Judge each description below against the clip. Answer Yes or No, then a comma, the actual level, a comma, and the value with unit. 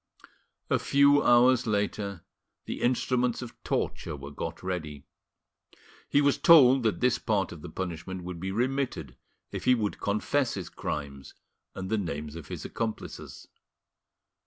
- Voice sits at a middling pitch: No, low, 105 Hz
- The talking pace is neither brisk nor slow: Yes, average, 145 wpm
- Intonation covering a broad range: Yes, wide, 6.9 semitones